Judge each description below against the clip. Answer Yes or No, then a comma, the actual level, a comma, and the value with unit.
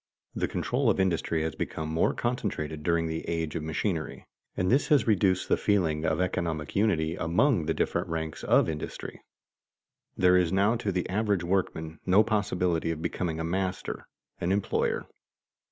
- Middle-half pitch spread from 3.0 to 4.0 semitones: Yes, average, 3.6 semitones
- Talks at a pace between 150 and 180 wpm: Yes, average, 170 wpm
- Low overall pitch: Yes, very low, 90 Hz